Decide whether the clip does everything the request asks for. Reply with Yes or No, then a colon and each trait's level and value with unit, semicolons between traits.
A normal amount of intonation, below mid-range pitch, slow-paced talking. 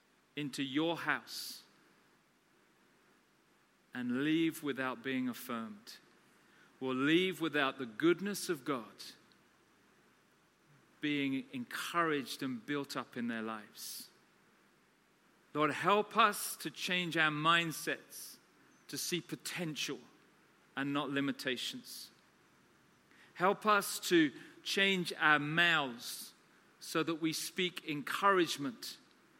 No: average, 4.9 semitones; medium, 155 Hz; slow, 95 wpm